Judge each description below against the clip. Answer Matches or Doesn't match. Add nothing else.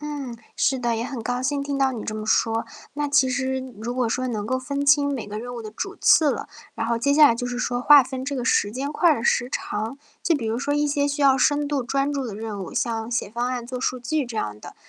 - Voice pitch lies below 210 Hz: Doesn't match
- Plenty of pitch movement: Doesn't match